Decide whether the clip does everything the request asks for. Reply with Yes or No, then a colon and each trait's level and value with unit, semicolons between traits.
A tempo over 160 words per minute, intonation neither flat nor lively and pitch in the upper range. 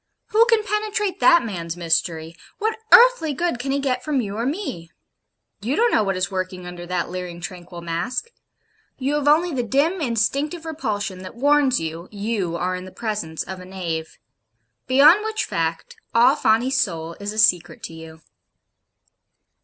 No: average, 170 wpm; wide, 8.8 semitones; high, 220 Hz